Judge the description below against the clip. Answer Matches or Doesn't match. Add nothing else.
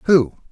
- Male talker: Matches